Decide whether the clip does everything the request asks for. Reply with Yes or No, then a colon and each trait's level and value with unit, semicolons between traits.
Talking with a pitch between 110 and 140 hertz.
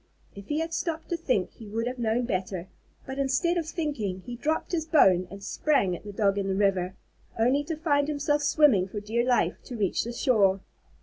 No: high, 240 Hz